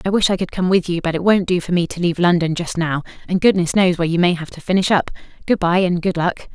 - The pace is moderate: No, fast, 305 wpm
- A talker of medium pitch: Yes, medium, 175 Hz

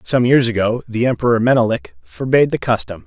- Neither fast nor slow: Yes, average, 175 wpm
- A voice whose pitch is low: Yes, low, 115 Hz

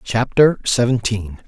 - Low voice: Yes, low, 115 Hz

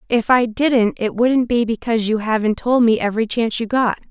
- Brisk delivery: Yes, fast, 220 wpm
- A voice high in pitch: Yes, high, 230 Hz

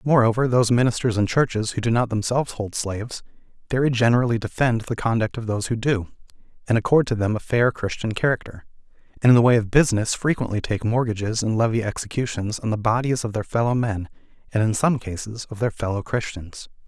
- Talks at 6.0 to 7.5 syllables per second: Yes, 6.2 syllables/s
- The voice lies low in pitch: Yes, low, 115 Hz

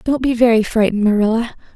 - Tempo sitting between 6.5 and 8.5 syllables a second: Yes, 6.8 syllables/s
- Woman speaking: Yes, female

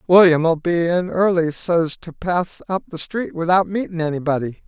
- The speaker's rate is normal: Yes, average, 165 wpm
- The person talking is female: No, male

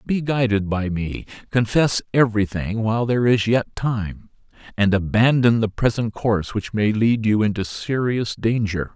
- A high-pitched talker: No, low, 110 Hz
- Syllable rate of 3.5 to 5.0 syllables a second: Yes, 4.6 syllables/s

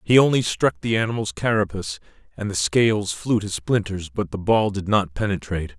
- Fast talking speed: No, average, 185 wpm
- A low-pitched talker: Yes, low, 100 Hz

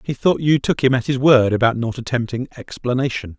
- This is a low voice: Yes, low, 125 Hz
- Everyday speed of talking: No, fast, 215 wpm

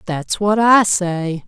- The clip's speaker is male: No, female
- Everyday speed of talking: Yes, average, 165 wpm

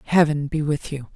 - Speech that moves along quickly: Yes, fast, 210 wpm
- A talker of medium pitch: Yes, medium, 150 Hz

